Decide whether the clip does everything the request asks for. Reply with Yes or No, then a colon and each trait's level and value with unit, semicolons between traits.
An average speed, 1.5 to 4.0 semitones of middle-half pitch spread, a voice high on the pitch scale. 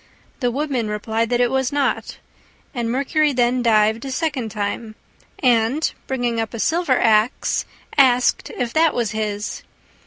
Yes: average, 150 wpm; average, 3.1 semitones; high, 245 Hz